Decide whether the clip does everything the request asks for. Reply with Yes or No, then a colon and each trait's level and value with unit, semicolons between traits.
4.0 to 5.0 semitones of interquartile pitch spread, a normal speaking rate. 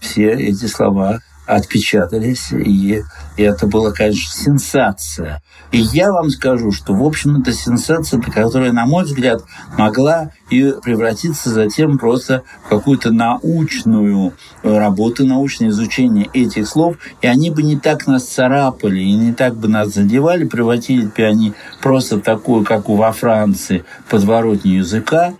Yes: average, 4.5 semitones; average, 140 wpm